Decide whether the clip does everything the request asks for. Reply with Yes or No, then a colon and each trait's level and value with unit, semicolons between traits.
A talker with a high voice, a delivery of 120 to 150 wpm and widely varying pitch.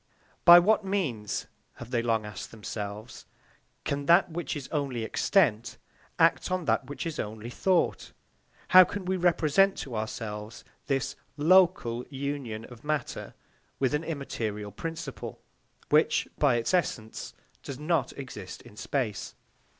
No: low, 135 Hz; slow, 135 wpm; wide, 6.7 semitones